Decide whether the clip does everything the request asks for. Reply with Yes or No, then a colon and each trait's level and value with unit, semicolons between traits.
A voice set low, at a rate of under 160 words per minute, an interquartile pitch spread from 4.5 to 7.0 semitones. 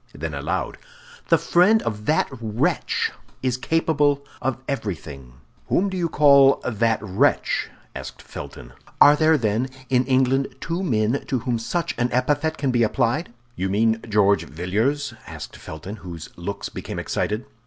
Yes: low, 125 Hz; average, 150 wpm; wide, 5.4 semitones